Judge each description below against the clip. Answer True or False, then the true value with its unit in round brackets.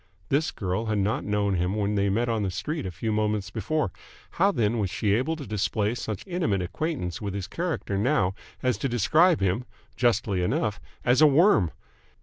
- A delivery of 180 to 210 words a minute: True (190 wpm)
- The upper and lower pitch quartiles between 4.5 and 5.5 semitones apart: True (5.1 semitones)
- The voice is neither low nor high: False (105 Hz)